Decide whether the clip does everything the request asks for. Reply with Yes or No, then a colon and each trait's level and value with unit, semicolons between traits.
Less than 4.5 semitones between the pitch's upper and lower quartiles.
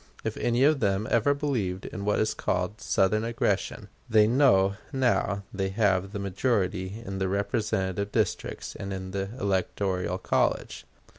Yes: average, 2.8 semitones